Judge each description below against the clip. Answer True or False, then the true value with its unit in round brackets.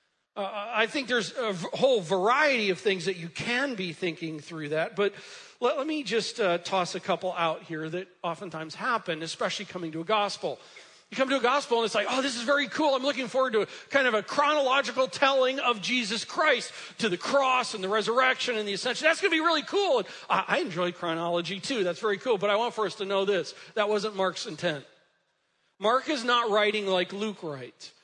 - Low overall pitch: False (215 Hz)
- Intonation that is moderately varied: False (6.1 semitones)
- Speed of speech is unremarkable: False (225 wpm)